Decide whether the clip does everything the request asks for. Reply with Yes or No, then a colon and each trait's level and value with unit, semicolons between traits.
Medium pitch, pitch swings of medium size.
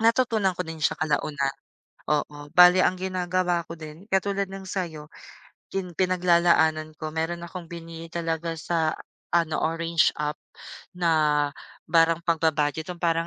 No: medium, 165 Hz; narrow, 2.3 semitones